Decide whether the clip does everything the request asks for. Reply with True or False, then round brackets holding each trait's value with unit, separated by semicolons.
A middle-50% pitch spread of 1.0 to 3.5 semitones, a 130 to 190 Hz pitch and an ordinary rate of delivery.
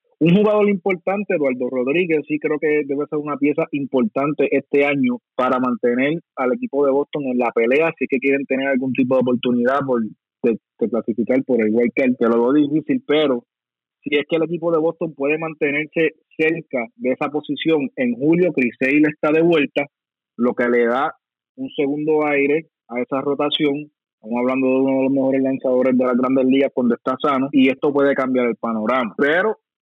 False (3.1 semitones; 140 Hz; 195 wpm)